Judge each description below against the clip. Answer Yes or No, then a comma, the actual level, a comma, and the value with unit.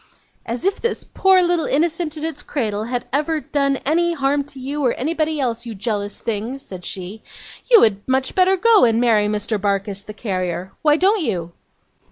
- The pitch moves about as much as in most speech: No, wide, 7.1 semitones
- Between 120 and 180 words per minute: No, average, 190 wpm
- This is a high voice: Yes, very high, 265 Hz